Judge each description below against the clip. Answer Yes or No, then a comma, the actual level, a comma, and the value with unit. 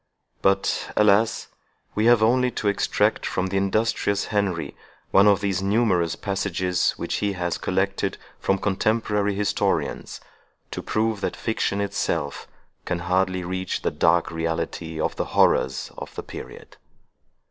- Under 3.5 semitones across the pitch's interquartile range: Yes, narrow, 2.5 semitones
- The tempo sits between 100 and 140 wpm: Yes, slow, 135 wpm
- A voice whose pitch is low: Yes, low, 100 Hz